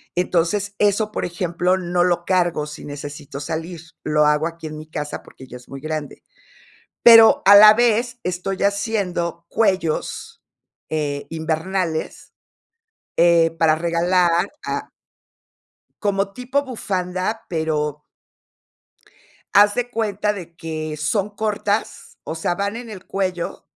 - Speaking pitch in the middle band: Yes, medium, 175 Hz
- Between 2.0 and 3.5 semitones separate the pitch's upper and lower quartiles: No, average, 4.3 semitones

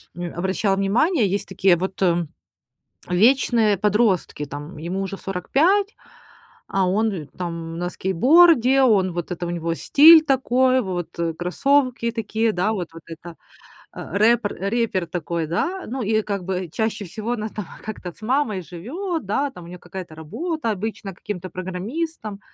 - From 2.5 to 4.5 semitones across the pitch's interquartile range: No, average, 5.2 semitones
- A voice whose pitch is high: Yes, high, 200 Hz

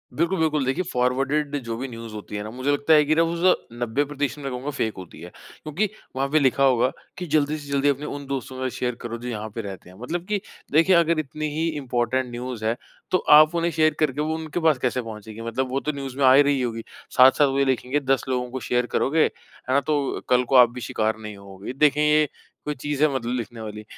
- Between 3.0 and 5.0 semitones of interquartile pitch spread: Yes, average, 3.8 semitones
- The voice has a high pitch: No, low, 135 Hz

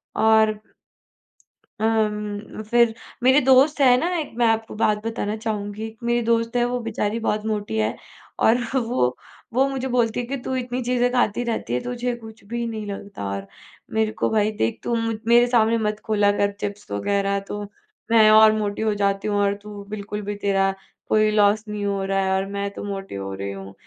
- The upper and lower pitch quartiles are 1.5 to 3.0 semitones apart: Yes, narrow, 2.5 semitones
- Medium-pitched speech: No, high, 215 Hz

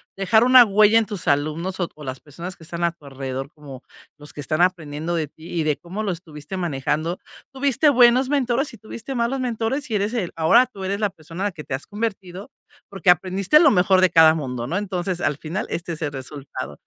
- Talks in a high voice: No, medium, 180 Hz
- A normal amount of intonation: No, wide, 5.9 semitones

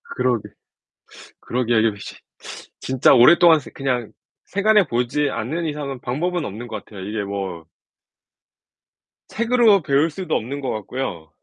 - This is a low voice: Yes, low, 130 Hz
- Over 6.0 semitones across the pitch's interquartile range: Yes, wide, 6.4 semitones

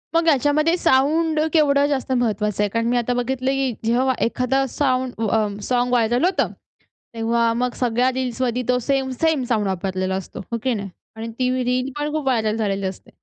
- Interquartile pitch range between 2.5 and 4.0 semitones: Yes, average, 3.1 semitones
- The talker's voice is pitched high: Yes, very high, 250 Hz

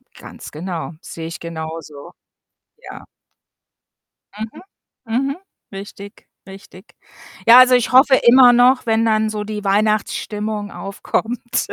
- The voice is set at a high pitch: Yes, high, 215 Hz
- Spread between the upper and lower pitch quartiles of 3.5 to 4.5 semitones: Yes, average, 3.8 semitones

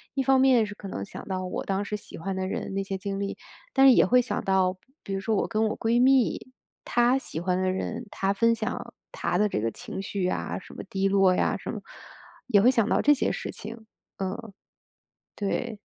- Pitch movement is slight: No, average, 3.4 semitones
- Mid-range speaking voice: No, high, 200 Hz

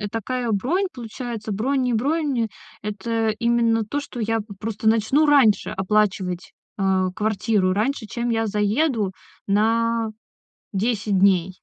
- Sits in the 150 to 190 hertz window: No, high, 220 Hz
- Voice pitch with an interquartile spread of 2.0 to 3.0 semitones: Yes, average, 2.7 semitones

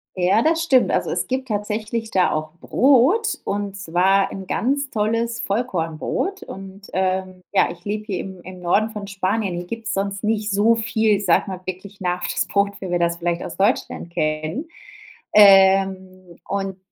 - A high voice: Yes, high, 195 Hz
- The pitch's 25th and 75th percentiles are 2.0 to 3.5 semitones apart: Yes, average, 3.1 semitones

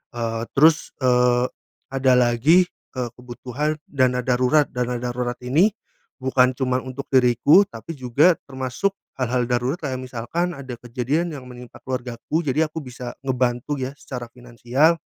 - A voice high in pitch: No, low, 125 Hz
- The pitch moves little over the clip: Yes, narrow, 2.1 semitones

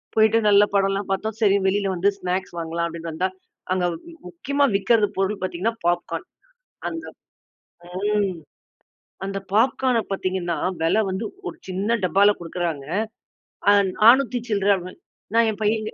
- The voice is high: Yes, high, 200 Hz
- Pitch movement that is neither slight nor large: Yes, average, 3.2 semitones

